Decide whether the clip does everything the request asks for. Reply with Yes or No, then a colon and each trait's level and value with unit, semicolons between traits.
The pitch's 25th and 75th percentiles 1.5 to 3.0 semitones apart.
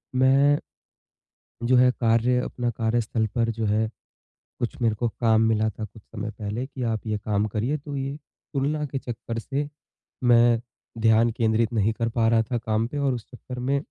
Yes: narrow, 2.4 semitones